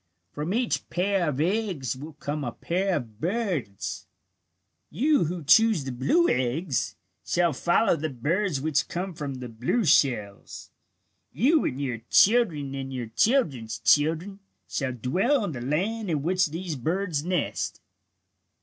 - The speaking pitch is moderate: Yes, medium, 155 Hz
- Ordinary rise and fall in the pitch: No, wide, 6.5 semitones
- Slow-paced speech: No, average, 145 wpm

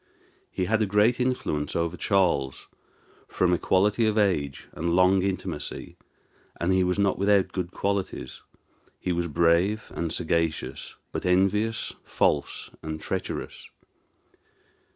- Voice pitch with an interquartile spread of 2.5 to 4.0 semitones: Yes, average, 3.0 semitones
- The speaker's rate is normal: No, slow, 120 wpm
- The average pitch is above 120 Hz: No, very low, 95 Hz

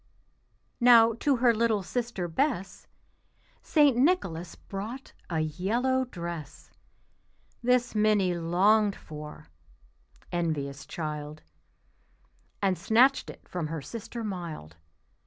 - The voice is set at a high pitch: Yes, high, 195 Hz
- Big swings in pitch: Yes, wide, 6.5 semitones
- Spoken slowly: Yes, slow, 100 wpm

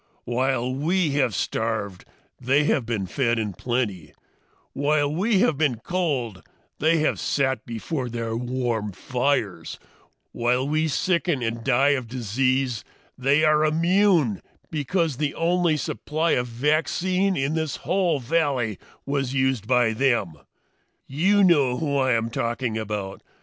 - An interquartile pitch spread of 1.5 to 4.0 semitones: No, average, 4.8 semitones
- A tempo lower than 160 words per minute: Yes, slow, 135 wpm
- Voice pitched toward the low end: Yes, low, 130 Hz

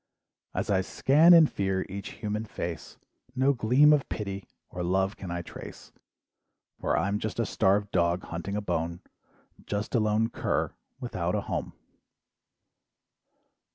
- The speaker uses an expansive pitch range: No, average, 3.3 semitones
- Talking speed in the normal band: Yes, average, 145 wpm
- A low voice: Yes, low, 100 Hz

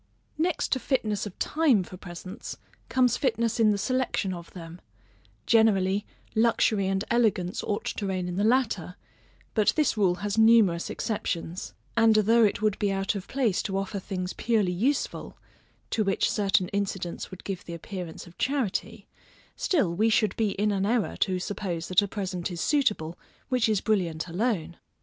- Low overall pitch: No, high, 200 Hz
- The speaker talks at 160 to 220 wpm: Yes, average, 170 wpm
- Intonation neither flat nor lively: Yes, average, 3.5 semitones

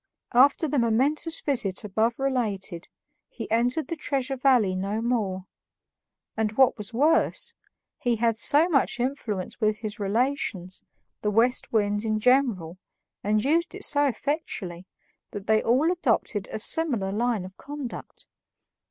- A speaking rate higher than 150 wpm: No, average, 140 wpm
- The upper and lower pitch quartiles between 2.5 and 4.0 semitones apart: No, average, 4.8 semitones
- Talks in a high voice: Yes, high, 230 Hz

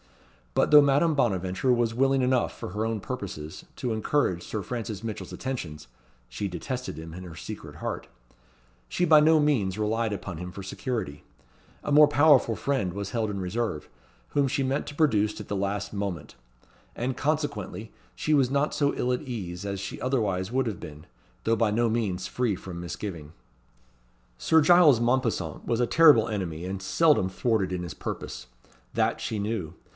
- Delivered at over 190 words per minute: No, average, 175 wpm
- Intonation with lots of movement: Yes, wide, 5.9 semitones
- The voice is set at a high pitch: No, low, 110 Hz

